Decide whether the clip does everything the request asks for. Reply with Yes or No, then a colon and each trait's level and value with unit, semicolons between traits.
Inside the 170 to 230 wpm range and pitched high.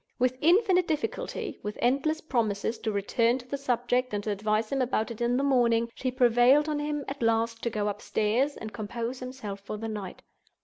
Yes: average, 195 wpm; high, 240 Hz